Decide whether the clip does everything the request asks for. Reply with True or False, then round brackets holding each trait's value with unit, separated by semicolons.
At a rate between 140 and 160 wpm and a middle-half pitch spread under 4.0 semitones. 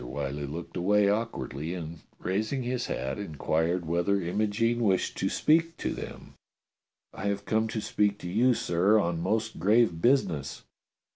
False (150 wpm; 4.8 semitones)